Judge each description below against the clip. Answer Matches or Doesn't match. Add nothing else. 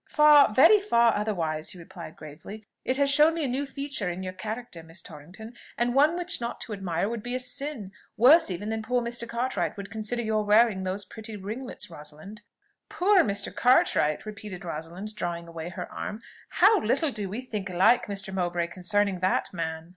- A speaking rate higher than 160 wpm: Matches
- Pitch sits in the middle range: Doesn't match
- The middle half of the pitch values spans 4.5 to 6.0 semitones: Matches